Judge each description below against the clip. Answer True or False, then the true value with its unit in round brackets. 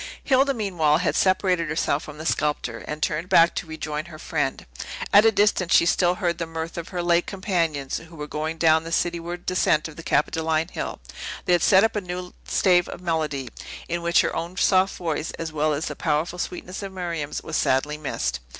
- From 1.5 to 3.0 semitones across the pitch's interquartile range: True (2.7 semitones)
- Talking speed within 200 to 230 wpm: True (205 wpm)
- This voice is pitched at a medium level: True (170 Hz)